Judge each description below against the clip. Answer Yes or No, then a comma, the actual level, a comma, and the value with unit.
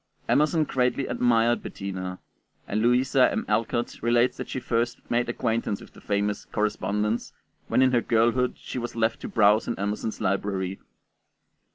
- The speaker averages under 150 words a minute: No, average, 155 wpm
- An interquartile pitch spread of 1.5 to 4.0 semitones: Yes, average, 2.8 semitones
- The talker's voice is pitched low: Yes, low, 115 Hz